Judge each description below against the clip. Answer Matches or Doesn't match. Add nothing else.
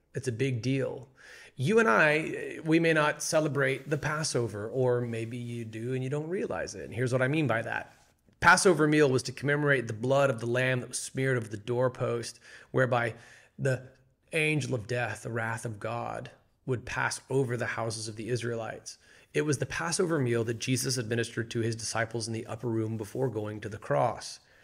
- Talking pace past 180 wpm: Matches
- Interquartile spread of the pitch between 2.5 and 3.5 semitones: Matches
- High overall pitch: Doesn't match